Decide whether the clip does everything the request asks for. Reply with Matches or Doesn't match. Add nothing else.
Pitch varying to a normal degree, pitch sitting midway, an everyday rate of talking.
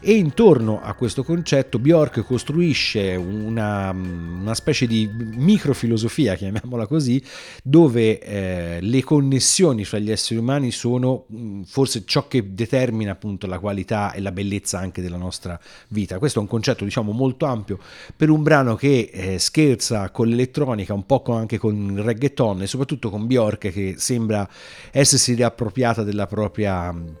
Doesn't match